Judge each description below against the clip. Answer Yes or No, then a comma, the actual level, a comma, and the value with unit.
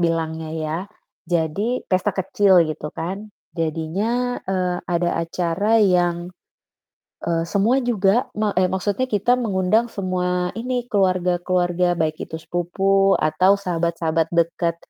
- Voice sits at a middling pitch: Yes, medium, 180 Hz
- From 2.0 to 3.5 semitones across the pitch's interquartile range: Yes, average, 3.0 semitones